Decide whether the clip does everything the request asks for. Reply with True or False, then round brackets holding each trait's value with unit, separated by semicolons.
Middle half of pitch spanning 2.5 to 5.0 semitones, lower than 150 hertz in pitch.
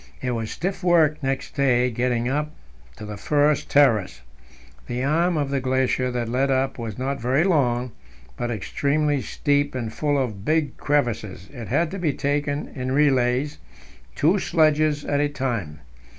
True (3.3 semitones; 135 Hz)